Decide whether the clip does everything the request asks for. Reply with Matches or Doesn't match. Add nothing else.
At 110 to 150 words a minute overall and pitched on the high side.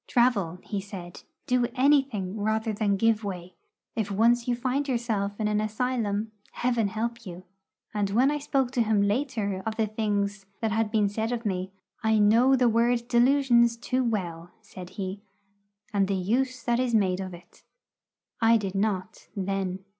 Doesn't match